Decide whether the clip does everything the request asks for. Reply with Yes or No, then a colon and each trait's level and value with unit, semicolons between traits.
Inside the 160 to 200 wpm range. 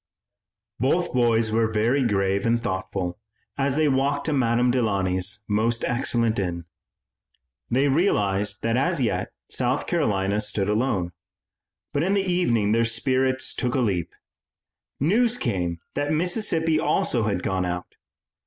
No: slow, 135 wpm